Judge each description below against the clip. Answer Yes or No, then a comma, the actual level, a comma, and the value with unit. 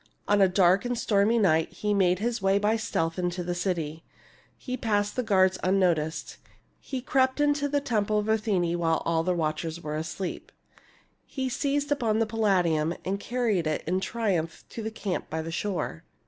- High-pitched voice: Yes, high, 195 Hz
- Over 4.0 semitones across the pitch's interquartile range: Yes, average, 4.7 semitones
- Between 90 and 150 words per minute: No, average, 180 wpm